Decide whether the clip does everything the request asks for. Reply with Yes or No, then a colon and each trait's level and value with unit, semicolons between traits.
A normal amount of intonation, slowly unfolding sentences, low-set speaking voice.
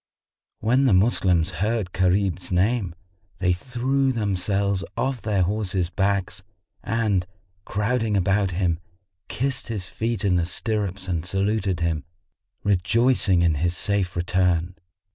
Yes: average, 3.4 semitones; slow, 125 wpm; very low, 95 Hz